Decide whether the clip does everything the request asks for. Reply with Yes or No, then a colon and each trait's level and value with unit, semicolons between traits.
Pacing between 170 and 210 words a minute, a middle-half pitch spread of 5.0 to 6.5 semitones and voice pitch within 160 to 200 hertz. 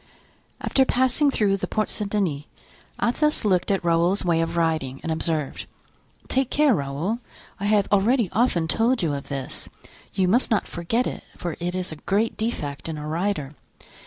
Yes: average, 175 wpm; wide, 5.6 semitones; medium, 185 Hz